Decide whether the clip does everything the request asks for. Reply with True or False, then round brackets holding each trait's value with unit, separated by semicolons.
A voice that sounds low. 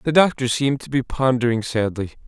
True (125 Hz)